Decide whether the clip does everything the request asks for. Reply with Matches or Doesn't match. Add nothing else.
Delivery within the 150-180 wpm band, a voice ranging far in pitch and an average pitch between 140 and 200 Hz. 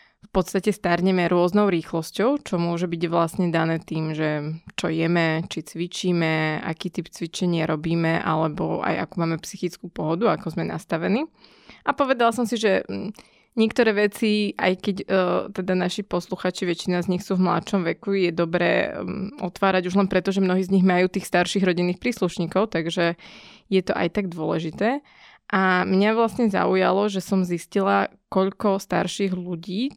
Doesn't match